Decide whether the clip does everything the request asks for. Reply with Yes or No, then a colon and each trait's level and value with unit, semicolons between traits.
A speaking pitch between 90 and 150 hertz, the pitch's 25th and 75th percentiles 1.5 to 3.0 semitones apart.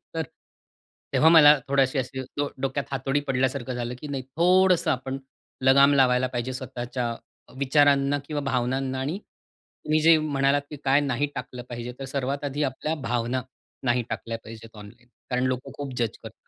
Yes: low, 135 Hz; narrow, 2.5 semitones